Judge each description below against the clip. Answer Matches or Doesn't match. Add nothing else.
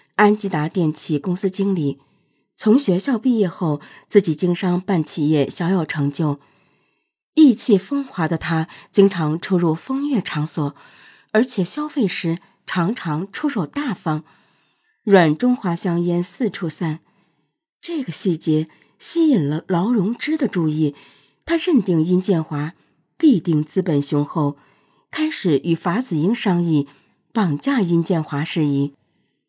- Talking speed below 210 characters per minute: Matches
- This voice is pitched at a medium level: Matches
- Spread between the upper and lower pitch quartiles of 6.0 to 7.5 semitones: Doesn't match